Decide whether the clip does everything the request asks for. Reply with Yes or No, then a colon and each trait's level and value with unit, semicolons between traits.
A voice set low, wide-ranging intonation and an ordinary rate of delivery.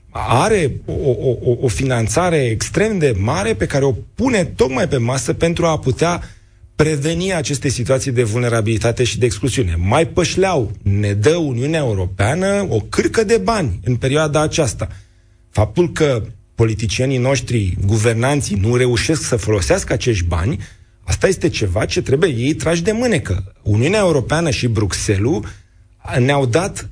Yes: low, 125 Hz; wide, 6.3 semitones; average, 145 wpm